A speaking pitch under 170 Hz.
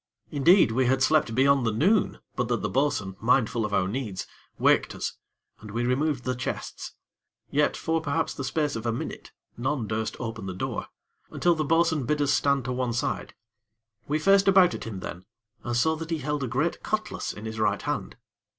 Yes: low, 135 Hz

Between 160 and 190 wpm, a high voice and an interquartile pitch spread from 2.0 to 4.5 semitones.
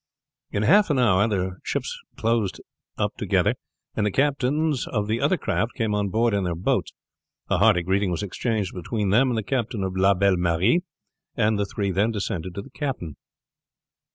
No: average, 185 wpm; low, 105 Hz; average, 3.9 semitones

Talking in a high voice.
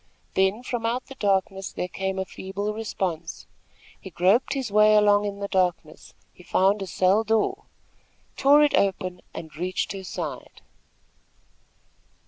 Yes: high, 195 Hz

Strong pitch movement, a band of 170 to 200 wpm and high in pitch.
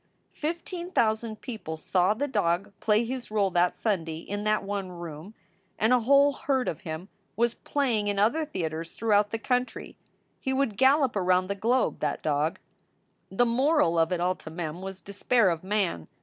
Yes: wide, 5.8 semitones; average, 180 wpm; high, 205 Hz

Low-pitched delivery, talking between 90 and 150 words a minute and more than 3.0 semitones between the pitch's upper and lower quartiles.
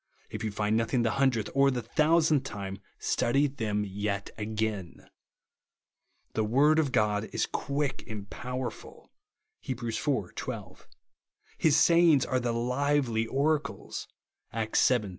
Yes: low, 120 Hz; average, 140 wpm; average, 4.6 semitones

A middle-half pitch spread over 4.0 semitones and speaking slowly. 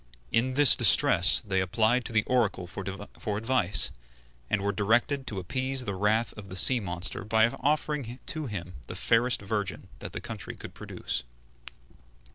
No: average, 4.4 semitones; average, 160 wpm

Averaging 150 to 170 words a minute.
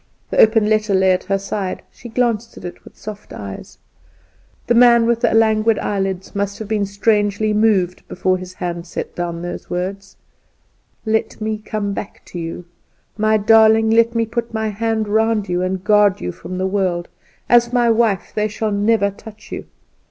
No: average, 185 wpm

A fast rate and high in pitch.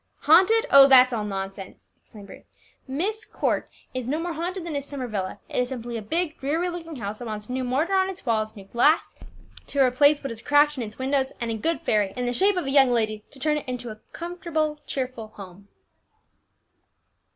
Yes: fast, 210 wpm; very high, 265 Hz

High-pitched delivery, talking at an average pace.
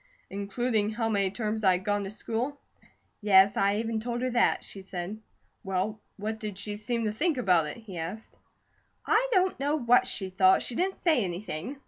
Yes: high, 215 Hz; average, 185 wpm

